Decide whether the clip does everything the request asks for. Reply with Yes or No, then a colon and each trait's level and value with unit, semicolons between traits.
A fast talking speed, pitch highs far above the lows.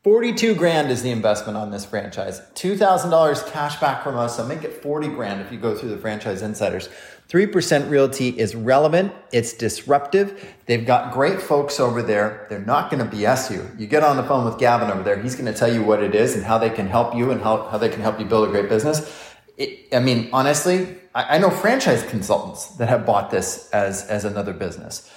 Yes: fast, 220 wpm; wide, 5.8 semitones